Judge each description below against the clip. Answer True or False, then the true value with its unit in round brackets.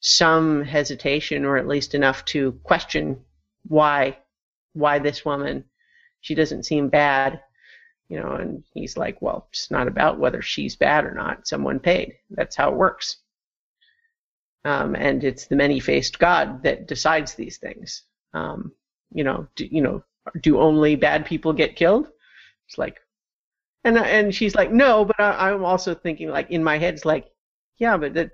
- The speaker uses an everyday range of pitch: False (6.1 semitones)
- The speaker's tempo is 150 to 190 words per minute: True (165 wpm)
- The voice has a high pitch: False (155 Hz)